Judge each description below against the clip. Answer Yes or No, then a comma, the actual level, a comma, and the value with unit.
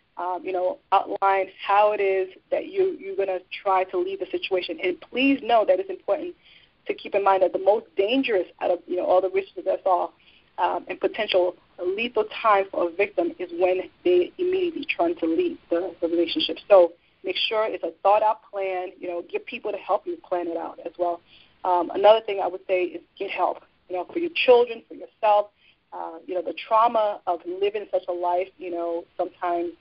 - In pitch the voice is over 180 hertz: Yes, high, 190 Hz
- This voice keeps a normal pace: No, fast, 215 wpm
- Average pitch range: Yes, average, 3.2 semitones